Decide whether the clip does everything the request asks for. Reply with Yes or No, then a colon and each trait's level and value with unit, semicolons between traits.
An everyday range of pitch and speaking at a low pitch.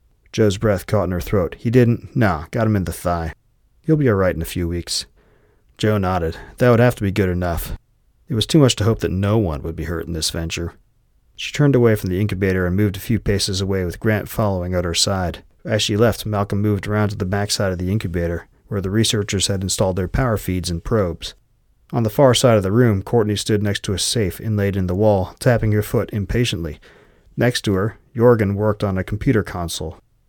Yes: average, 3.6 semitones; low, 100 Hz